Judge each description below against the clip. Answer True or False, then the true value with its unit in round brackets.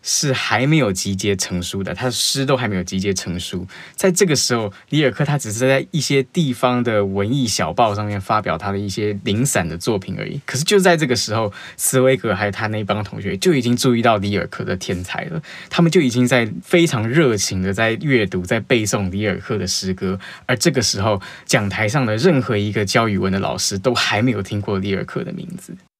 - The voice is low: True (110 Hz)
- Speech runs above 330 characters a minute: False (325 characters per minute)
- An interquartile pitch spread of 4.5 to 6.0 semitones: True (5.1 semitones)